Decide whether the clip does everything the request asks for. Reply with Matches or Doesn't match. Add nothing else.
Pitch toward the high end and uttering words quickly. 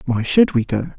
Doesn't match